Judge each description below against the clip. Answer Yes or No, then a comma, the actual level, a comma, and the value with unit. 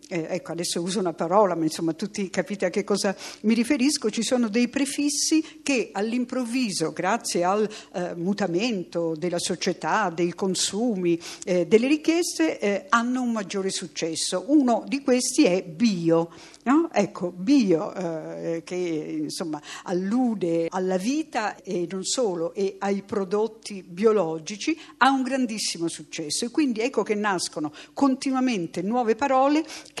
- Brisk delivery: No, average, 140 wpm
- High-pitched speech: Yes, high, 200 Hz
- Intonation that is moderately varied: No, wide, 6.0 semitones